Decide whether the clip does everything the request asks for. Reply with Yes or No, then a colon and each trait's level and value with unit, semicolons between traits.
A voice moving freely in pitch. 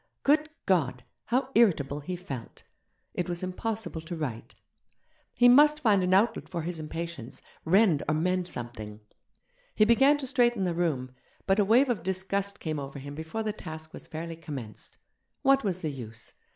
Yes: wide, 6.3 semitones